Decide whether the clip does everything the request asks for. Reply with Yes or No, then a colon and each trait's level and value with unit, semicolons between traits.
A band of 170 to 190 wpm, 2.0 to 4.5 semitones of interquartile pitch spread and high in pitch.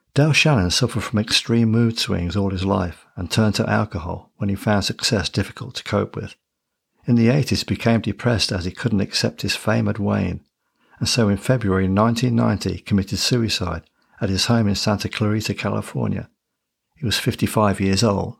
No: average, 180 wpm; average, 2.8 semitones; low, 105 Hz